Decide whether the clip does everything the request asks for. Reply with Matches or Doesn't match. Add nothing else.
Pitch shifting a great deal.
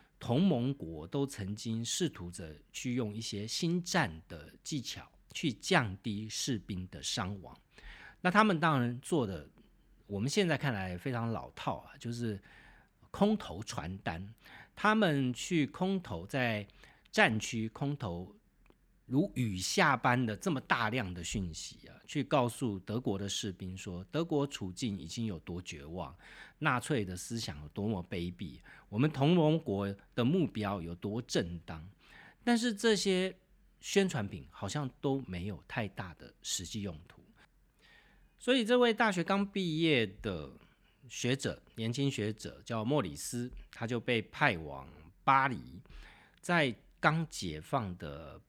Matches